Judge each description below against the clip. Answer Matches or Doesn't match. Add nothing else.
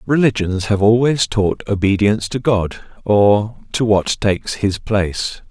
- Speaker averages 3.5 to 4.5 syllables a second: Matches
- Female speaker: Doesn't match